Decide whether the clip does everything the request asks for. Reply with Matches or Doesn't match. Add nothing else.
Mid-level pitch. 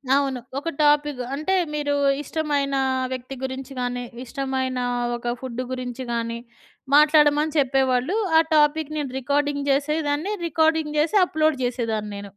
Doesn't match